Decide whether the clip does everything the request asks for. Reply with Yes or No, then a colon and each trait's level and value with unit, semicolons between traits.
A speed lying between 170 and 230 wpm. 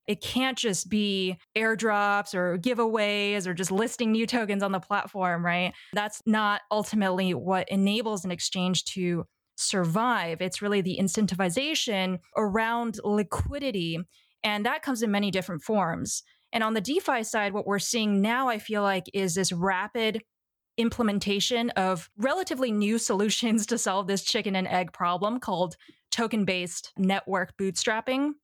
No: average, 150 wpm